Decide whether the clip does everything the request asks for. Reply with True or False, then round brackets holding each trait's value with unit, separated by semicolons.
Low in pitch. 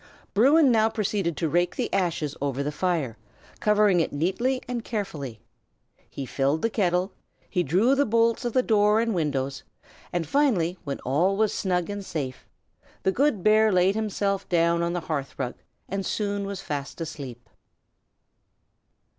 False (185 Hz)